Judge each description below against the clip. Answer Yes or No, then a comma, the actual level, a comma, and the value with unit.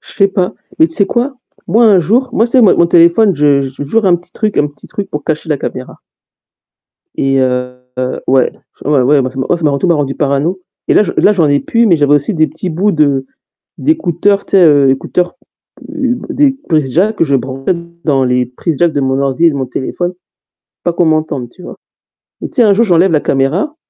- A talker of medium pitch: Yes, medium, 160 Hz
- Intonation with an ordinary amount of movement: No, wide, 5.9 semitones